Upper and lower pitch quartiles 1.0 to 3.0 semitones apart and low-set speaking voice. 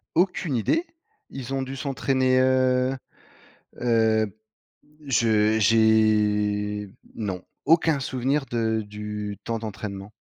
No: average, 3.8 semitones; low, 115 Hz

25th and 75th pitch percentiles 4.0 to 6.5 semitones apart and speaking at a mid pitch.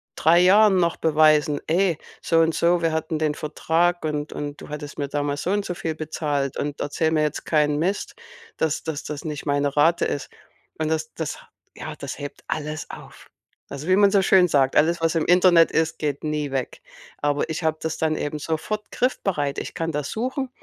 No: narrow, 2.5 semitones; medium, 155 Hz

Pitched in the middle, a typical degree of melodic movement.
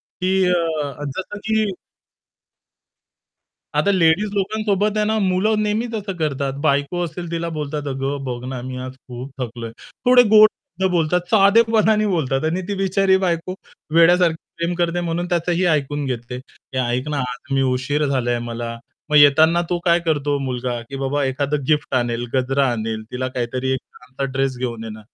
No: medium, 150 Hz; wide, 5.9 semitones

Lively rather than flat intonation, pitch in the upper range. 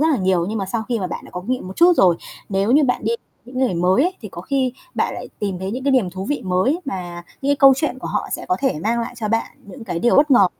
Yes: wide, 6.1 semitones; high, 225 Hz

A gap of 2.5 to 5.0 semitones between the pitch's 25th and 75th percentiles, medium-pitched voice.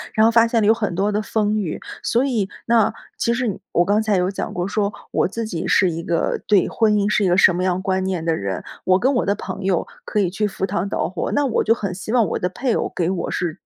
No: average, 3.3 semitones; high, 200 Hz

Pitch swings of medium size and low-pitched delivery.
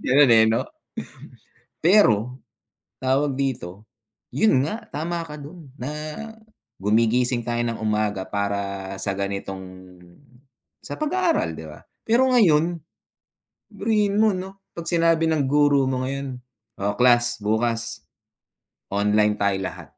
No: wide, 7.6 semitones; low, 130 Hz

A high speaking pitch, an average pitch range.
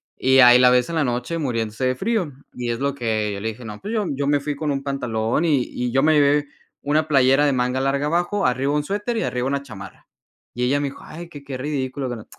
No: low, 135 Hz; average, 3.0 semitones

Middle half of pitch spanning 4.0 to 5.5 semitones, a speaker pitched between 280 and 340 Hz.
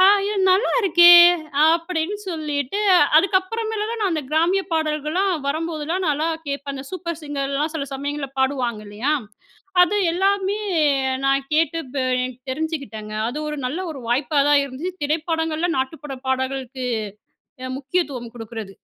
Yes: average, 4.3 semitones; very high, 300 Hz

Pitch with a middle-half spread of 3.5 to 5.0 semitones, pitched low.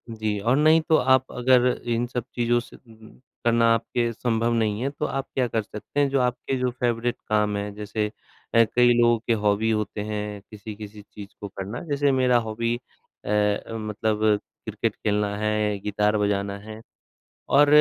No: average, 2.7 semitones; low, 110 Hz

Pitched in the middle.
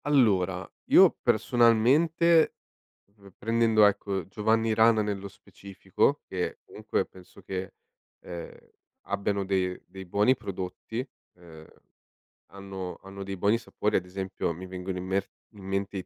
No: low, 100 Hz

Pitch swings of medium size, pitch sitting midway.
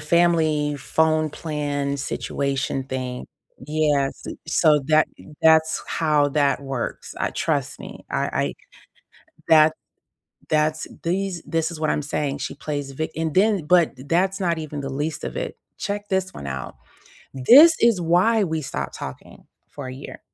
Yes: average, 3.2 semitones; medium, 155 Hz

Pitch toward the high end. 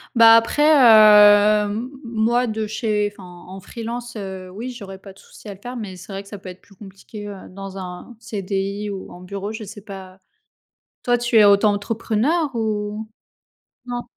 Yes: high, 210 Hz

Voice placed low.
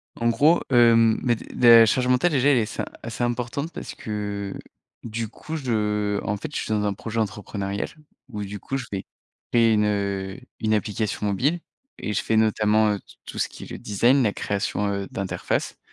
Yes: low, 110 Hz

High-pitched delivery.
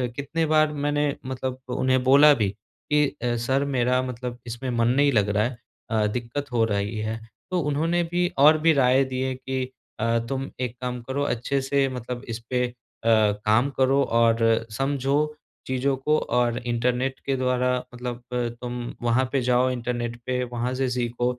No: low, 125 Hz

